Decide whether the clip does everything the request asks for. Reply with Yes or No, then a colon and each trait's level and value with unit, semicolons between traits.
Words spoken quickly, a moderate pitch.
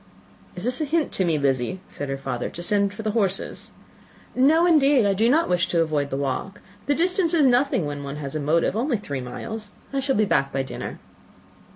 No: fast, 220 wpm; high, 200 Hz